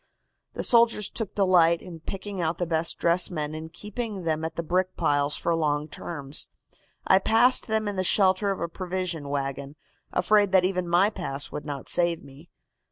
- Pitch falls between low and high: Yes, medium, 175 Hz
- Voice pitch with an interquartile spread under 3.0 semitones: No, average, 3.7 semitones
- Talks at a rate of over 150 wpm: Yes, average, 185 wpm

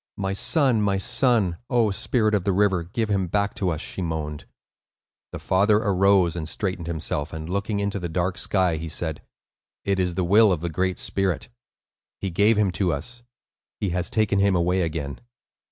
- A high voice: No, very low, 95 Hz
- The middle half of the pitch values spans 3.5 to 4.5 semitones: No, average, 3.0 semitones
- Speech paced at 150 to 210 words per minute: Yes, average, 185 wpm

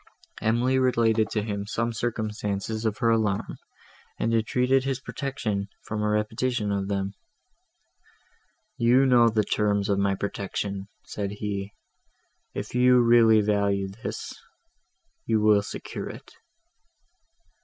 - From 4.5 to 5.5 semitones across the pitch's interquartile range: No, narrow, 2.6 semitones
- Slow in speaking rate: Yes, slow, 125 wpm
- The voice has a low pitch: Yes, low, 110 Hz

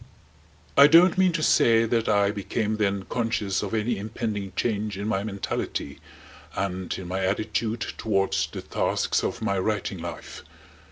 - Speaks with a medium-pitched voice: No, low, 105 Hz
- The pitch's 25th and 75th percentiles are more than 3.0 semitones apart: No, narrow, 2.6 semitones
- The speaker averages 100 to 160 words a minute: Yes, average, 155 wpm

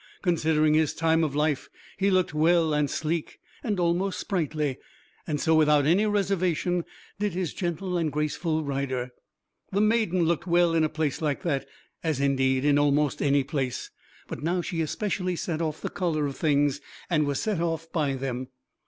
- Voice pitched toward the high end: No, medium, 160 Hz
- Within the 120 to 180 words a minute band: Yes, average, 175 wpm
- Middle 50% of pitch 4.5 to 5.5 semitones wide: No, average, 3.3 semitones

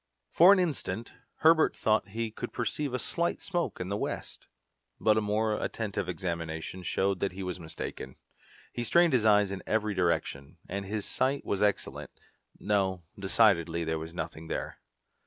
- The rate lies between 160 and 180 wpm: Yes, average, 165 wpm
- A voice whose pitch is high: No, low, 100 Hz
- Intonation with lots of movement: No, average, 4.3 semitones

